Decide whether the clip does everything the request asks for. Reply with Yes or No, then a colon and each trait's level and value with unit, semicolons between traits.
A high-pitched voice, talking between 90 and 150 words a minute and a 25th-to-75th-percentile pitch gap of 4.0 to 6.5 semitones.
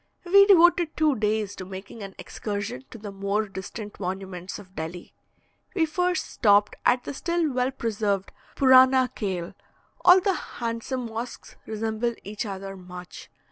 Yes: high, 220 Hz; average, 145 wpm; average, 5.0 semitones